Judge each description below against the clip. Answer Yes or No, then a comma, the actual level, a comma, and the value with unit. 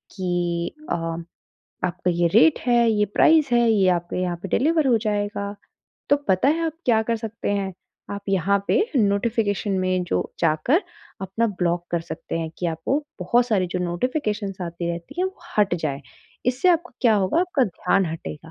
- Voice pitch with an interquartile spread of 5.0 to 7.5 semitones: Yes, average, 5.3 semitones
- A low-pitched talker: No, high, 200 Hz